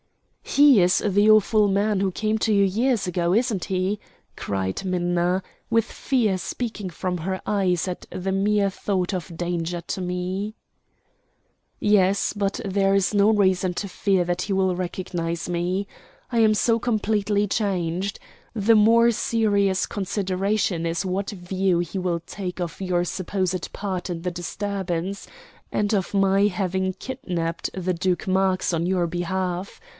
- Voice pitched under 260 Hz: Yes, high, 190 Hz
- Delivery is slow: No, average, 150 wpm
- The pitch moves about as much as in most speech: No, narrow, 2.3 semitones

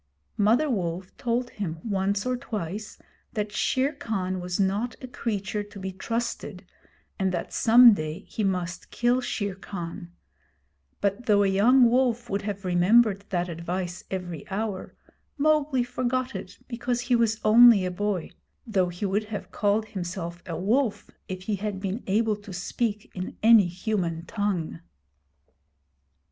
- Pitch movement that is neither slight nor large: Yes, average, 4.0 semitones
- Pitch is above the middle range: Yes, high, 205 Hz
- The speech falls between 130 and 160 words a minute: Yes, average, 150 wpm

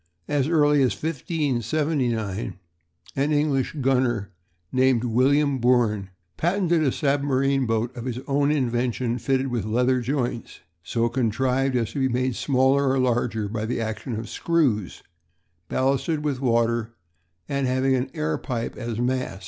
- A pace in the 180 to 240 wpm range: No, average, 140 wpm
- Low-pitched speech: Yes, low, 130 Hz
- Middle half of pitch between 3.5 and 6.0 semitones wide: No, average, 2.9 semitones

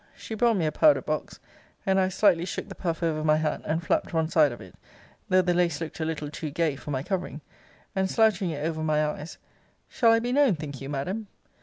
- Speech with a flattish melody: No, average, 3.8 semitones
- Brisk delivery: Yes, fast, 230 wpm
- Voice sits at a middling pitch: Yes, medium, 165 Hz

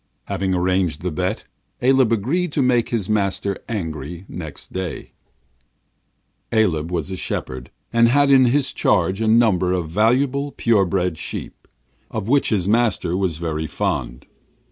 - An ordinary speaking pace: Yes, average, 145 wpm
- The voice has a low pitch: Yes, low, 100 Hz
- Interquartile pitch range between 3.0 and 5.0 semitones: No, wide, 5.4 semitones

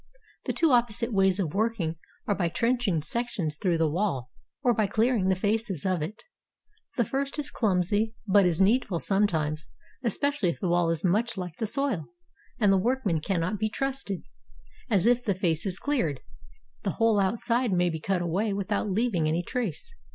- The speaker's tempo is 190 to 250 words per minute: No, average, 175 wpm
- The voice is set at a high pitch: Yes, high, 200 Hz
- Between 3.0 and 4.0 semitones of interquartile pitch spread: No, average, 4.9 semitones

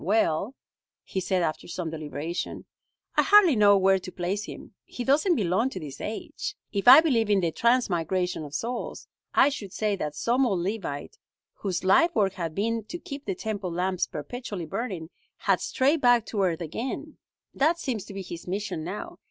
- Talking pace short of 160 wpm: No, average, 185 wpm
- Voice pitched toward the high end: Yes, high, 200 Hz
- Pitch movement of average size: No, wide, 5.7 semitones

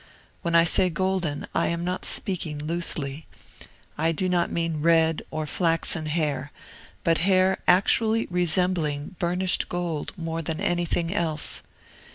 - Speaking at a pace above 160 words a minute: No, slow, 135 wpm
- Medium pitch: Yes, medium, 170 Hz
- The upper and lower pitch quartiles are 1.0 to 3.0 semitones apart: Yes, narrow, 2.4 semitones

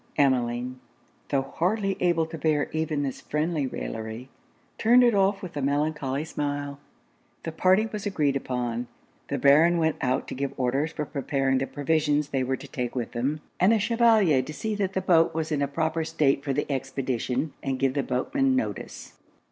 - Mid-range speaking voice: Yes, medium, 145 Hz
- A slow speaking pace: No, average, 185 wpm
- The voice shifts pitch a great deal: No, average, 3.8 semitones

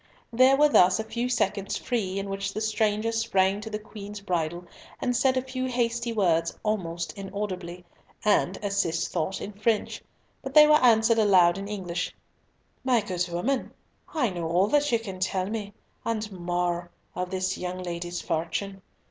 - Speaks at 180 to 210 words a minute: No, average, 170 wpm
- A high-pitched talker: Yes, high, 200 Hz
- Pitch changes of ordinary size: Yes, average, 4.0 semitones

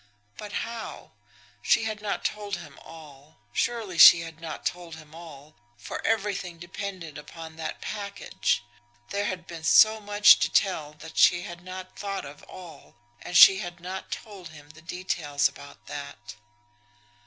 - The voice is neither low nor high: Yes, medium, 175 Hz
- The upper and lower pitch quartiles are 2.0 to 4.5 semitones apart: Yes, average, 4.0 semitones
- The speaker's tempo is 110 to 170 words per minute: Yes, average, 155 wpm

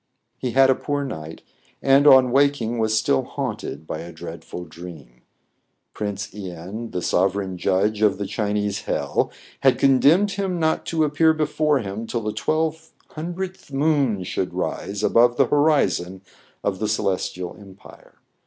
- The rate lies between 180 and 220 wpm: No, average, 155 wpm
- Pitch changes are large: Yes, wide, 7.2 semitones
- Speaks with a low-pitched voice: Yes, low, 110 Hz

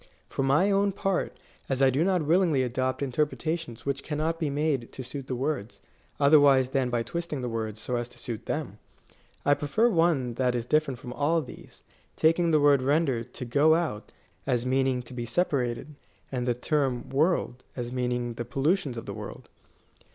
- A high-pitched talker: No, low, 135 Hz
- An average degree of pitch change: Yes, average, 4.1 semitones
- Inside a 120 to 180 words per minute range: No, average, 190 wpm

